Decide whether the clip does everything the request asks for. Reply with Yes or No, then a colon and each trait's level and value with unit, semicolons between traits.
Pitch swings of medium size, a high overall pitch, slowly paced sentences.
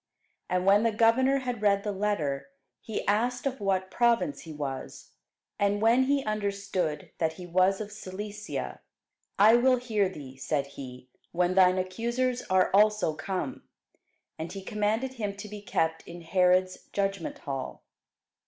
No: average, 3.7 semitones; high, 200 Hz; average, 155 wpm